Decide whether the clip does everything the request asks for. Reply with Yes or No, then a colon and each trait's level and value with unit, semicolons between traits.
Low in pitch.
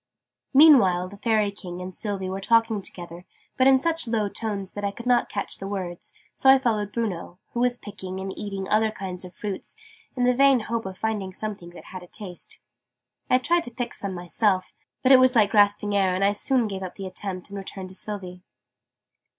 No: high, 205 Hz